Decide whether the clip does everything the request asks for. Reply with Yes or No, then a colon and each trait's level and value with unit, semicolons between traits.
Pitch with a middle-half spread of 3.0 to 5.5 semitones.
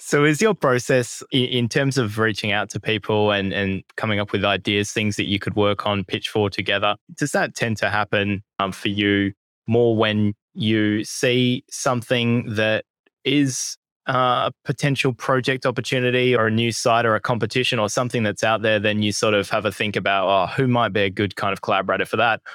Yes: average, 3.4 semitones